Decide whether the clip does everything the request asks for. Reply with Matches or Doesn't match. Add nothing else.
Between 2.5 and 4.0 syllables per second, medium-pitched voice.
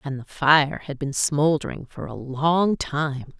Matches